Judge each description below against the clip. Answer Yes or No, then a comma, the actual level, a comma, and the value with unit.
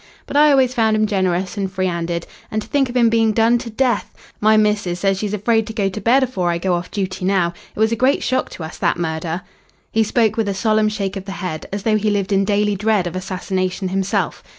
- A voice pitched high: Yes, high, 205 Hz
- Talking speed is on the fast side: Yes, fast, 250 wpm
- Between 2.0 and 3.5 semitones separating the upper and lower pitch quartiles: Yes, average, 3.1 semitones